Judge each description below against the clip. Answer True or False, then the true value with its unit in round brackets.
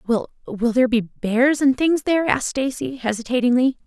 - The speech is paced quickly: False (155 wpm)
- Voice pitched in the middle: False (250 Hz)